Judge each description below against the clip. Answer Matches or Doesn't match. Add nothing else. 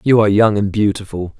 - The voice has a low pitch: Matches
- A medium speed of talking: Doesn't match